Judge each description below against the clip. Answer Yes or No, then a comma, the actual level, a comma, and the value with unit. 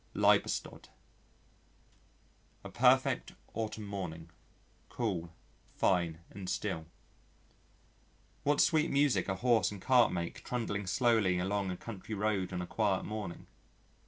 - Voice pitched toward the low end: Yes, low, 100 Hz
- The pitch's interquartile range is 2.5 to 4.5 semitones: Yes, average, 3.9 semitones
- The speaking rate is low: Yes, slow, 115 wpm